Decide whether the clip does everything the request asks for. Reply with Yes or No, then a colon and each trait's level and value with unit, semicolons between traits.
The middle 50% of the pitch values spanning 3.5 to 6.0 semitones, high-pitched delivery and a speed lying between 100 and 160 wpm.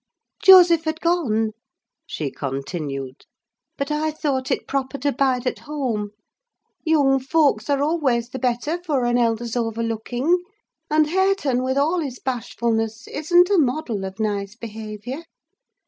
Yes: wide, 5.4 semitones; very high, 260 Hz; slow, 135 wpm